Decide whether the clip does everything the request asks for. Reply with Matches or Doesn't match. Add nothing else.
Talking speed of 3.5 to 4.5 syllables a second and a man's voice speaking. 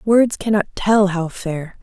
Doesn't match